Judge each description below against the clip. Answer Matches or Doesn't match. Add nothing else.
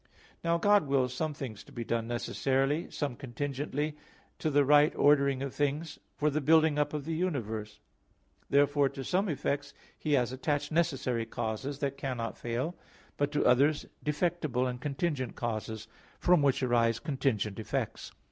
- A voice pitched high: Doesn't match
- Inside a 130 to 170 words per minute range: Matches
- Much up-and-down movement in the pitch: Doesn't match